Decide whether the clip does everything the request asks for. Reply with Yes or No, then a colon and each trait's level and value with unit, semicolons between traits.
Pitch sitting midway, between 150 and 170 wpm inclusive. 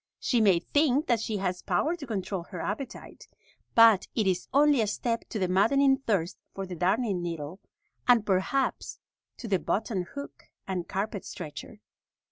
No: high, 205 Hz; average, 165 wpm